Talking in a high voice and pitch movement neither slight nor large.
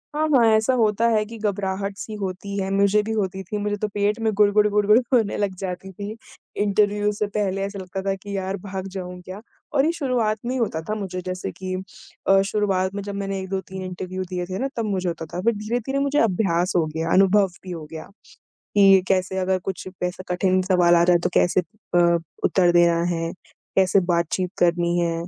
No: high, 195 Hz; narrow, 2.3 semitones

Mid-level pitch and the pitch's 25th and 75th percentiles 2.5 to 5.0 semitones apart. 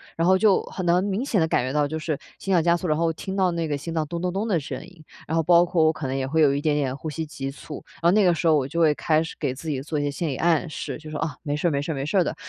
Yes: medium, 160 Hz; average, 2.8 semitones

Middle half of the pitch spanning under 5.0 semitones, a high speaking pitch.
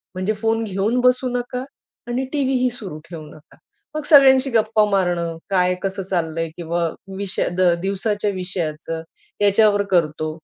No: average, 5.3 semitones; high, 195 Hz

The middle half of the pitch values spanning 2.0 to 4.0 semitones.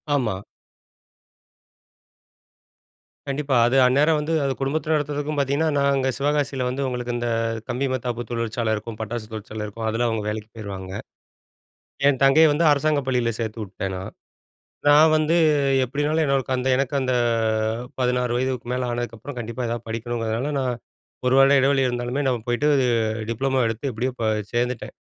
Yes: average, 3.2 semitones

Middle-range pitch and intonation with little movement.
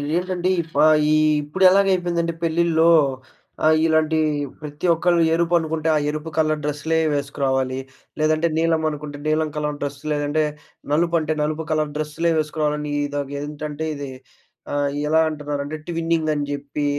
Yes: medium, 155 Hz; narrow, 1.9 semitones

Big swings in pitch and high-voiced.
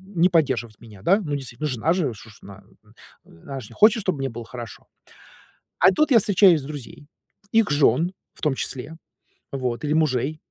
No: wide, 6.1 semitones; medium, 145 Hz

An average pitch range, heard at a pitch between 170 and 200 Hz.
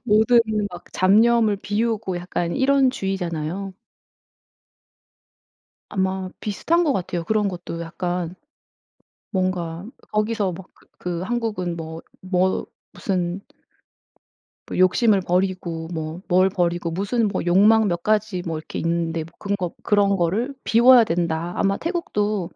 Yes: average, 3.6 semitones; high, 190 Hz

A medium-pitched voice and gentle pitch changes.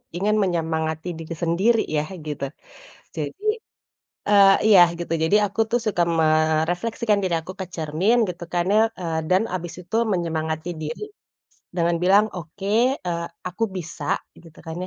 No: medium, 175 Hz; average, 3.4 semitones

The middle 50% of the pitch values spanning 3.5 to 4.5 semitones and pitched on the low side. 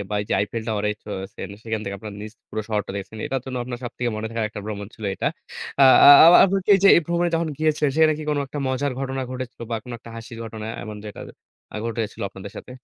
Yes: average, 4.2 semitones; low, 115 Hz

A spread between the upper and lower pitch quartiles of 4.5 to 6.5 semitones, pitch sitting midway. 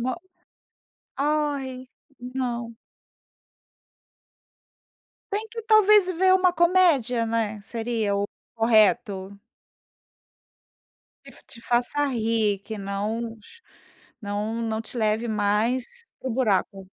No: average, 5.1 semitones; high, 235 Hz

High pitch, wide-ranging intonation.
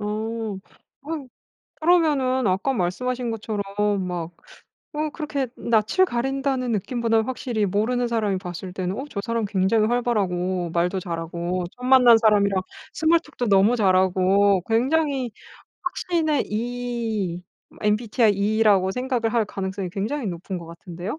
No: high, 220 Hz; average, 4.7 semitones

